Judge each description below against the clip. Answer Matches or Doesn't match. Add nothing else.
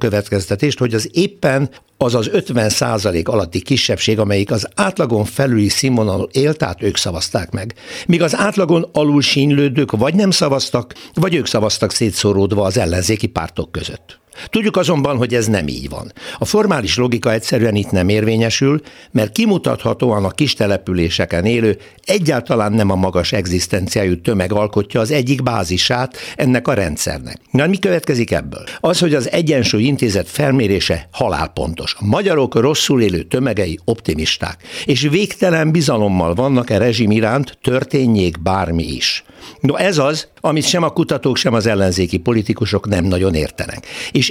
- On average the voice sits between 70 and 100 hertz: Doesn't match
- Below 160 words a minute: Matches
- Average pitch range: Doesn't match